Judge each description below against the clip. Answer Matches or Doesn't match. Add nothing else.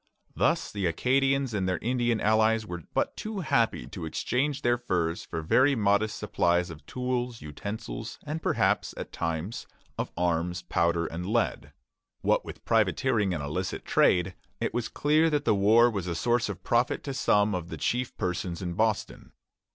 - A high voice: Doesn't match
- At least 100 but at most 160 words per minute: Doesn't match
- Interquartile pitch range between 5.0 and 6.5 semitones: Matches